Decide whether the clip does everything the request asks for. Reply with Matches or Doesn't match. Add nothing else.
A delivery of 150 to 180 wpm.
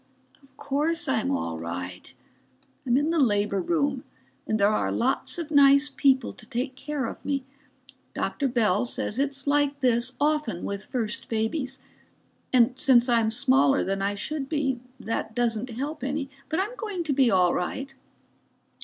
Matches